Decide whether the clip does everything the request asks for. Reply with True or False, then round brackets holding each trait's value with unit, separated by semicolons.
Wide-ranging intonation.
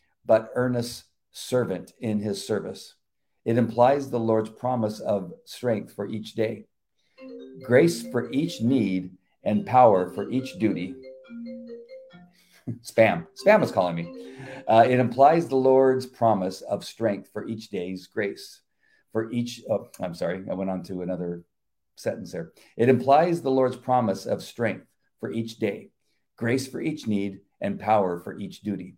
False (5.0 semitones)